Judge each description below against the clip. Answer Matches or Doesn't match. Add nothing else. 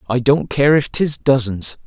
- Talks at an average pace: Matches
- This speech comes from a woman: Doesn't match